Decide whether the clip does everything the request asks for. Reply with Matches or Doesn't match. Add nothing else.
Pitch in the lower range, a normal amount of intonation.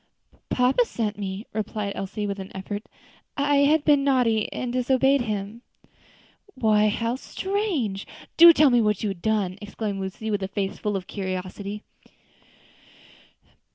Doesn't match